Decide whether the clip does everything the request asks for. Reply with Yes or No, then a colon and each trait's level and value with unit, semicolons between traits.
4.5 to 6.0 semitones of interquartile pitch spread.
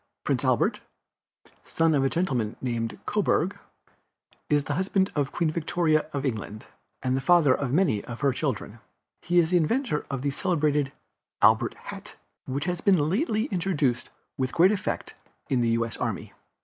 Yes: average, 5.2 semitones